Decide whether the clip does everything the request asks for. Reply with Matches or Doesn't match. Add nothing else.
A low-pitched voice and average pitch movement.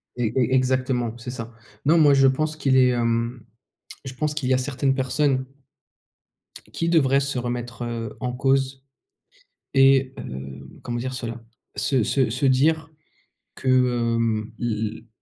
Doesn't match